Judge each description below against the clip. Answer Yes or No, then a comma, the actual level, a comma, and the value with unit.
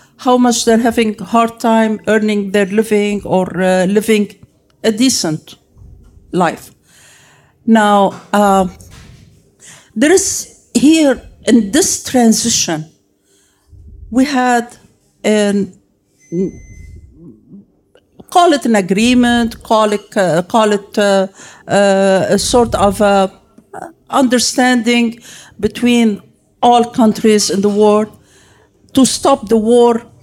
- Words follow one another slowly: Yes, slow, 105 wpm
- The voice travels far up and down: No, average, 3.5 semitones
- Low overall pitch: No, high, 215 Hz